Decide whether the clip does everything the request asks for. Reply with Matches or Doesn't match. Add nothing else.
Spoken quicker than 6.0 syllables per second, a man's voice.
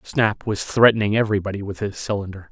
Matches